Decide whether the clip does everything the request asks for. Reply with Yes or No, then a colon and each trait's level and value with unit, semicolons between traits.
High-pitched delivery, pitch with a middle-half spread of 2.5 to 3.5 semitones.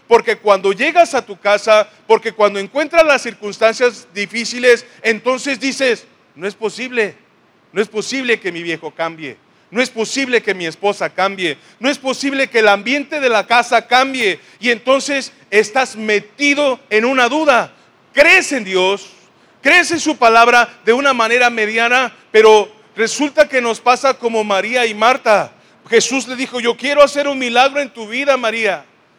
No: high, 235 Hz; average, 4.0 semitones